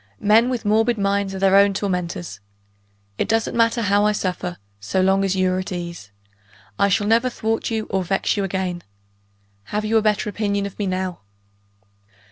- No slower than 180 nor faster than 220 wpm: Yes, average, 185 wpm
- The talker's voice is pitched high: Yes, high, 200 Hz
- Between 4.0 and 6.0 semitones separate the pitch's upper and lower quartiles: No, narrow, 2.4 semitones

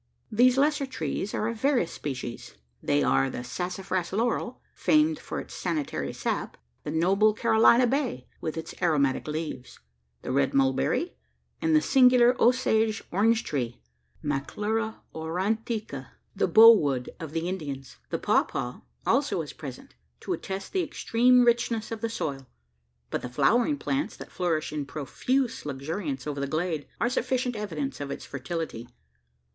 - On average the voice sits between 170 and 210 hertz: Yes, medium, 185 Hz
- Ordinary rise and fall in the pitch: No, wide, 8.3 semitones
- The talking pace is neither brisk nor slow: Yes, average, 150 wpm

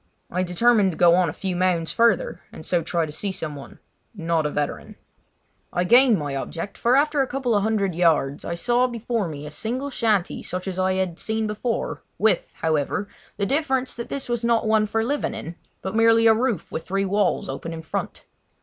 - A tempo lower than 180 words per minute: No, fast, 205 wpm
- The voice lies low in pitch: No, high, 200 Hz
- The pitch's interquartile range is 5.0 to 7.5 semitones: Yes, average, 5.3 semitones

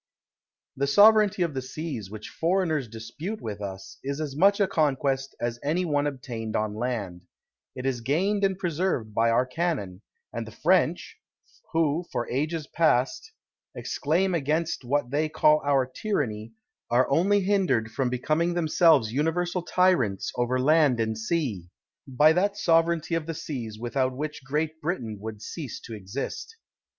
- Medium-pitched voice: Yes, medium, 145 Hz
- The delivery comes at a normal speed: Yes, average, 155 wpm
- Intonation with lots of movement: Yes, wide, 6.0 semitones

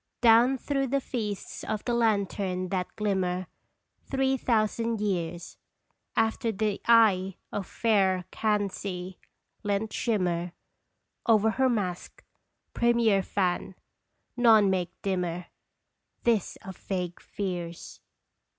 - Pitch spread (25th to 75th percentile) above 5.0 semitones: No, average, 3.7 semitones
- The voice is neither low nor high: No, high, 205 Hz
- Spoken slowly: Yes, slow, 105 wpm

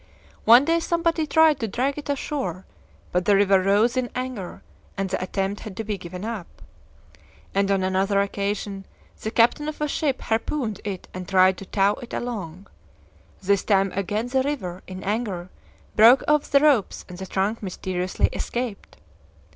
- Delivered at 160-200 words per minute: Yes, average, 170 wpm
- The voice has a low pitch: No, high, 205 Hz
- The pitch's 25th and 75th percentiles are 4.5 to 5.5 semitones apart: Yes, average, 5.0 semitones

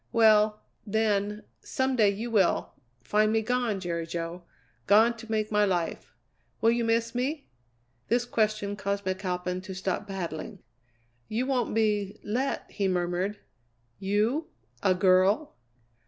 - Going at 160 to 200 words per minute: No, slow, 135 wpm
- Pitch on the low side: No, high, 210 Hz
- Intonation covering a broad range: No, average, 3.1 semitones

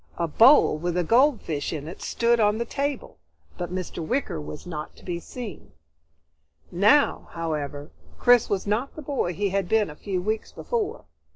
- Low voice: No, high, 200 Hz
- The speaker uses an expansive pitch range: Yes, wide, 6.4 semitones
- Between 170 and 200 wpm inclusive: Yes, average, 175 wpm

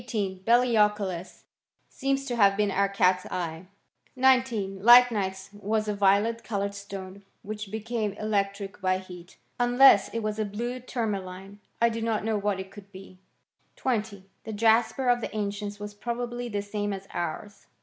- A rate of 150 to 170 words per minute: Yes, average, 160 wpm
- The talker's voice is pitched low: No, high, 205 Hz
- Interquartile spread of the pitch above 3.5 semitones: No, average, 2.7 semitones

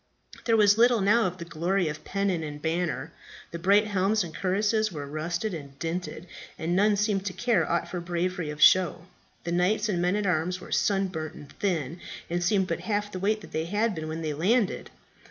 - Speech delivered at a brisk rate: Yes, fast, 210 wpm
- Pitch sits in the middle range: Yes, medium, 180 Hz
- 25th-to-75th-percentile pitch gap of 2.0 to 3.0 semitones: No, average, 3.9 semitones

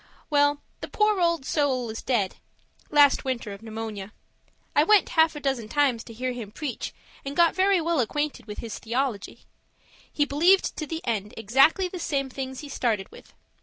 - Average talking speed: Yes, average, 180 wpm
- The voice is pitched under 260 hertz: No, very high, 270 Hz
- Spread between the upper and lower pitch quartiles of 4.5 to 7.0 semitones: Yes, average, 5.2 semitones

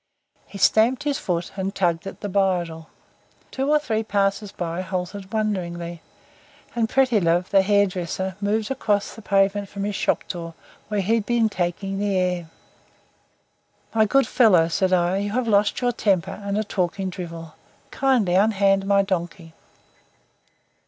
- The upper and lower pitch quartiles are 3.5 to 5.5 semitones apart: No, average, 3.1 semitones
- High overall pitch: Yes, high, 195 Hz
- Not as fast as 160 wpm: Yes, average, 150 wpm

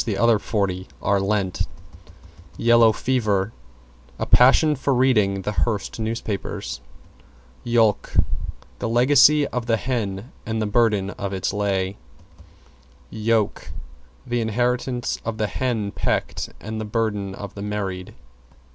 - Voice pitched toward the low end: Yes, low, 110 Hz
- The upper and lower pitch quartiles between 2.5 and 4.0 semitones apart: Yes, average, 3.2 semitones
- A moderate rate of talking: No, slow, 110 wpm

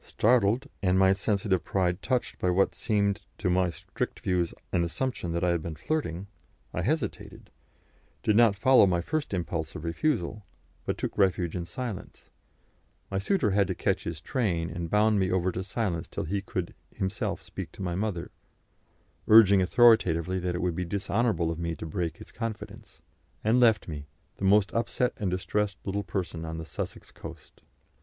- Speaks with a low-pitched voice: Yes, very low, 95 Hz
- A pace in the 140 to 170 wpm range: No, average, 180 wpm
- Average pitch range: Yes, average, 3.7 semitones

